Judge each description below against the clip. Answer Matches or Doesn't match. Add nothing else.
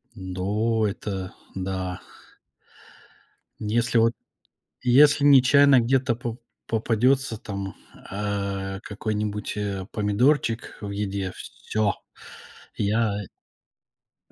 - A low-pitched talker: Matches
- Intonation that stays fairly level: Doesn't match